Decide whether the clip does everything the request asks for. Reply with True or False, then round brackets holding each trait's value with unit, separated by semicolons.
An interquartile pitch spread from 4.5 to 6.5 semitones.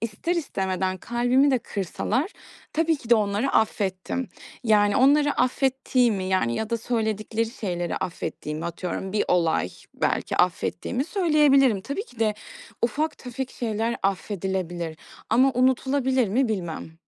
True (5.6 semitones)